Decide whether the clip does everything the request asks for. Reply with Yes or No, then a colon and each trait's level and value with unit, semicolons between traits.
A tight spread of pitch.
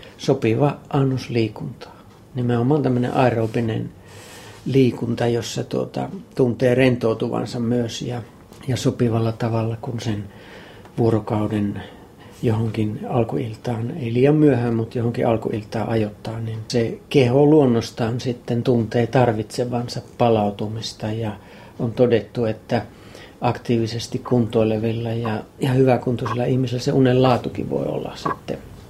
Yes: narrow, 2.1 semitones